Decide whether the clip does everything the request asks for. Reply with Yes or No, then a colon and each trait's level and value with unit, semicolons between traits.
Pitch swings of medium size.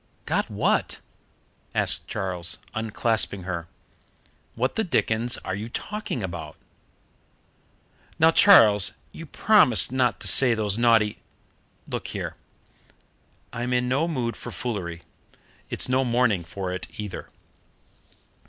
Yes: average, 4.7 semitones